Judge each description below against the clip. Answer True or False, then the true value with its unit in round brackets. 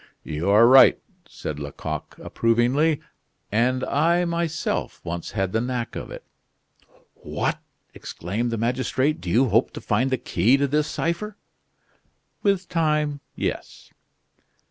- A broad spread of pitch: True (5.8 semitones)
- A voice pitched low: True (130 Hz)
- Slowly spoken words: True (130 wpm)